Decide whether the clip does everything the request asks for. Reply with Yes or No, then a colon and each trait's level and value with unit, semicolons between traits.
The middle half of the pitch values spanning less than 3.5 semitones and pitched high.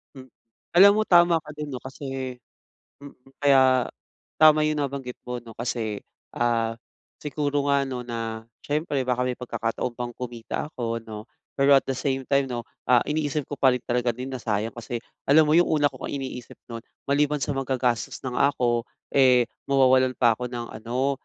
No: average, 2.9 semitones; low, 130 Hz